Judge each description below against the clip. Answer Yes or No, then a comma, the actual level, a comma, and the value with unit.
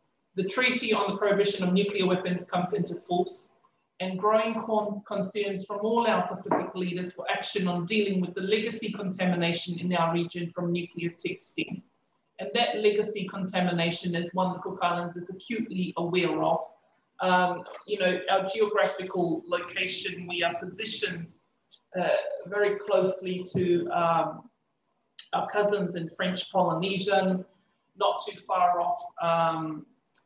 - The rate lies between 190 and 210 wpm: No, average, 145 wpm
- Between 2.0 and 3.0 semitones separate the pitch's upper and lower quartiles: Yes, narrow, 2.5 semitones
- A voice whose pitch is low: No, medium, 185 Hz